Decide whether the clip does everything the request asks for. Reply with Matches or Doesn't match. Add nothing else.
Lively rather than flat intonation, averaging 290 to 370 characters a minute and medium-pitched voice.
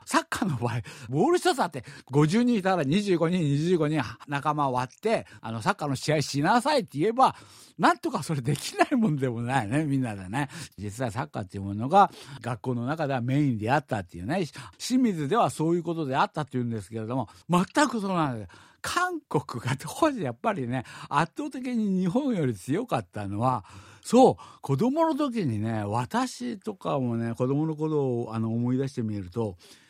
Matches